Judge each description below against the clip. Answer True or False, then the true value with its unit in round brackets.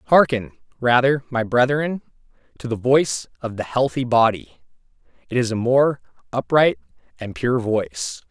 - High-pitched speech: False (120 Hz)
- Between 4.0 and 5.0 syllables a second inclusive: True (4.5 syllables/s)